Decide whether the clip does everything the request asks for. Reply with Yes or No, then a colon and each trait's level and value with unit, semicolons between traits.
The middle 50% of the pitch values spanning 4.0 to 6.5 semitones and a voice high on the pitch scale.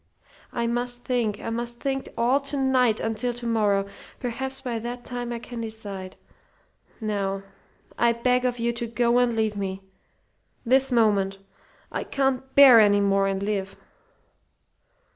No: average, 3.0 semitones; high, 235 Hz